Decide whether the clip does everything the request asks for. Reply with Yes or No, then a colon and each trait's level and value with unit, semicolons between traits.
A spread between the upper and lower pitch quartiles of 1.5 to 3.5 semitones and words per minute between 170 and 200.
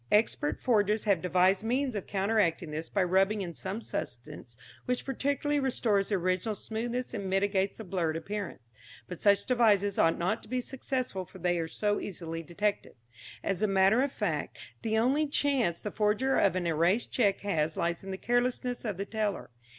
No: average, 4.1 semitones; average, 180 wpm